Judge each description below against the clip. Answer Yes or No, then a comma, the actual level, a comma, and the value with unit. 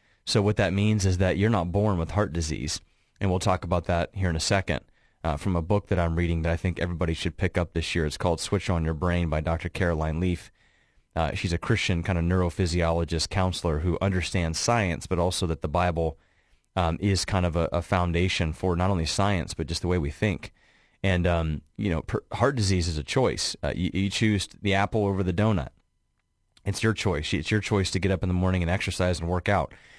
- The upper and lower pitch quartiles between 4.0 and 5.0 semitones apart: No, average, 2.7 semitones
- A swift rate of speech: Yes, fast, 230 wpm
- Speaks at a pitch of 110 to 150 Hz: No, very low, 90 Hz